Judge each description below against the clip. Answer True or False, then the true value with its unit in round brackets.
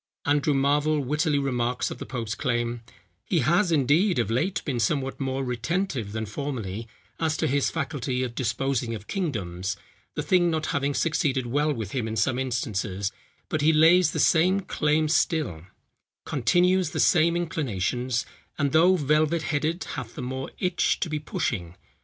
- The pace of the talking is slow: False (165 wpm)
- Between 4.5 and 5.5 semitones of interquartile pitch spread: True (4.9 semitones)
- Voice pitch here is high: False (140 Hz)